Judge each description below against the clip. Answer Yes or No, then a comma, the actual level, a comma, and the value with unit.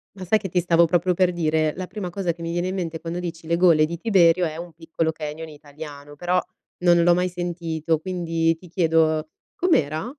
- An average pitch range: No, narrow, 1.9 semitones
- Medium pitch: Yes, medium, 170 Hz